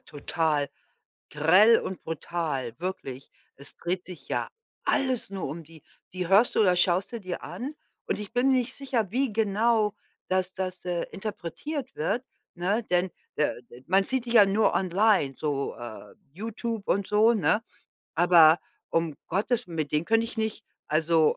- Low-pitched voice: No, medium, 185 Hz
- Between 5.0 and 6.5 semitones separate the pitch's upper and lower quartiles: Yes, wide, 5.4 semitones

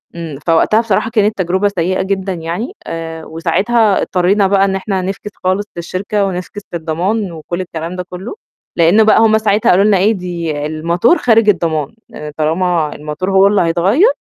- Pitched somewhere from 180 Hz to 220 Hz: Yes, medium, 185 Hz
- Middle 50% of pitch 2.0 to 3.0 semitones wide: No, average, 3.6 semitones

